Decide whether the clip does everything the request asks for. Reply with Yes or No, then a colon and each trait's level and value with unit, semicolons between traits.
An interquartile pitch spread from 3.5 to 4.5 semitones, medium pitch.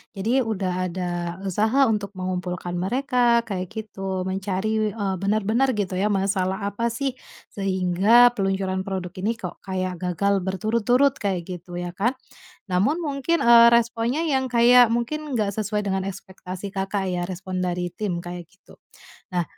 No: average, 3.9 semitones; high, 195 Hz